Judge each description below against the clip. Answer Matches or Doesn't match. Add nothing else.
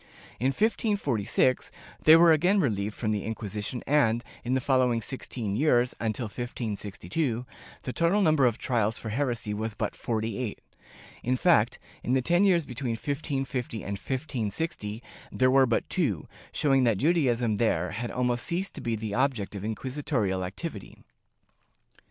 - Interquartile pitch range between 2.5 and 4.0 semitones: Doesn't match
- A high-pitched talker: Doesn't match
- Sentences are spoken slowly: Doesn't match